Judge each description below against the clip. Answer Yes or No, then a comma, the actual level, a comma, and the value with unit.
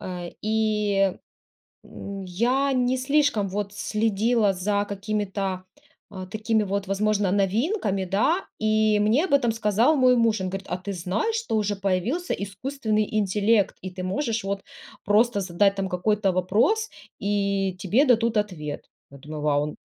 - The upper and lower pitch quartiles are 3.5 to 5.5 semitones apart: No, average, 2.9 semitones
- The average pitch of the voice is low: No, high, 205 Hz